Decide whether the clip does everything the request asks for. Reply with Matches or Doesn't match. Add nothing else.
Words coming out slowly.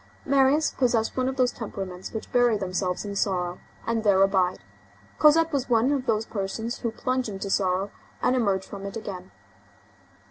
Doesn't match